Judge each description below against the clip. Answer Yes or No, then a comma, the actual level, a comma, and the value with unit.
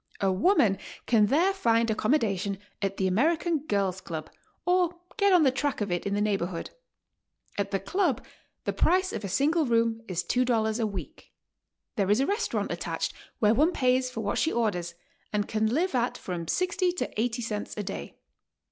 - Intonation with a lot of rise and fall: Yes, wide, 7.2 semitones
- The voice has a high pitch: Yes, high, 225 Hz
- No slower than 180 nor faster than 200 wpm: Yes, average, 185 wpm